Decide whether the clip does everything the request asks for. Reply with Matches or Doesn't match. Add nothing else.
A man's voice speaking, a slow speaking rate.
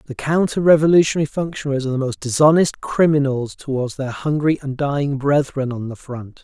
Doesn't match